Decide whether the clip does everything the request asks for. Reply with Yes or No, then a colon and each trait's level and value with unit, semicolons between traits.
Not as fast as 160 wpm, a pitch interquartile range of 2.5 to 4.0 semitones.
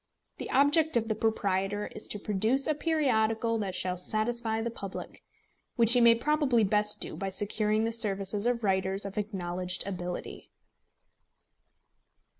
Yes: average, 145 wpm; average, 3.2 semitones